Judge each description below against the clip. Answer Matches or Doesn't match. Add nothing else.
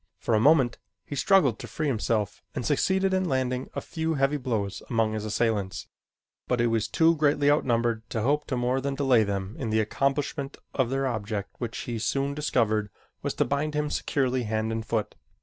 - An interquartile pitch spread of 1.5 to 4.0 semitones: Doesn't match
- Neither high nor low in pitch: Doesn't match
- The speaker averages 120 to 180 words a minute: Doesn't match